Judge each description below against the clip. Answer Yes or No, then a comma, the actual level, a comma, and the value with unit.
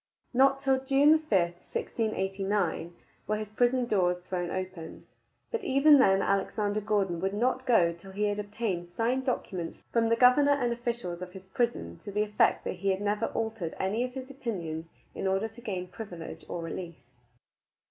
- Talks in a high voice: Yes, high, 205 Hz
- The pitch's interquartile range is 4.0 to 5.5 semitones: Yes, average, 4.9 semitones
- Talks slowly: No, average, 175 wpm